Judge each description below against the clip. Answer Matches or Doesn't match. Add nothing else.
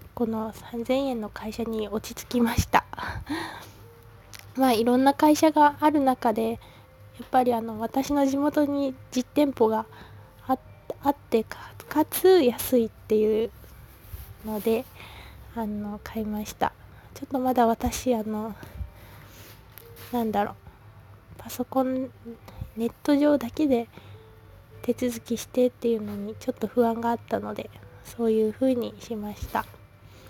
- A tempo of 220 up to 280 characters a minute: Matches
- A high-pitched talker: Matches